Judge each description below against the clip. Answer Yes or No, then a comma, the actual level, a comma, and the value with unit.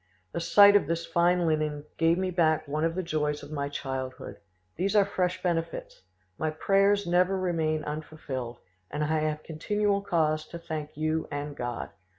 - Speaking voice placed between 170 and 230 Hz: No, medium, 160 Hz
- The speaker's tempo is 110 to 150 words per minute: No, average, 170 wpm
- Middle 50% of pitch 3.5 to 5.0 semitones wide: No, average, 3.0 semitones